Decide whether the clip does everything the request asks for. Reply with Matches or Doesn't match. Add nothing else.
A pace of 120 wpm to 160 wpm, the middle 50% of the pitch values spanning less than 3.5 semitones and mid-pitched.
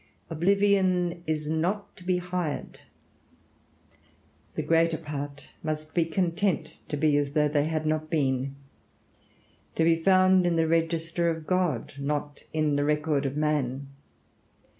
Matches